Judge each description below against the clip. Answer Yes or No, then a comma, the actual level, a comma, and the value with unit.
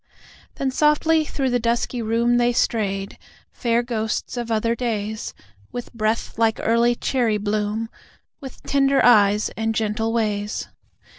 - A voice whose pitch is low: No, high, 230 Hz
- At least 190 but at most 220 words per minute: No, slow, 135 wpm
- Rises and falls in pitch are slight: Yes, narrow, 2.0 semitones